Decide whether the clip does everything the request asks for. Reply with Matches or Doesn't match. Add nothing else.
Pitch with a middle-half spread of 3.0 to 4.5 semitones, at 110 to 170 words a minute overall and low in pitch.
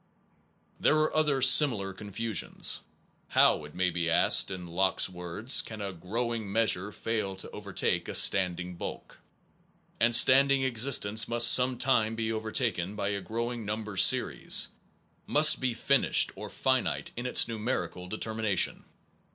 Matches